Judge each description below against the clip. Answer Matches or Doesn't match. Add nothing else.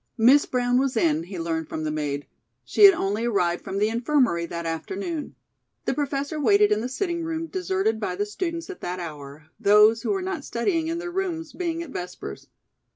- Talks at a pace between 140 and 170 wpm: Doesn't match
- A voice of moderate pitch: Doesn't match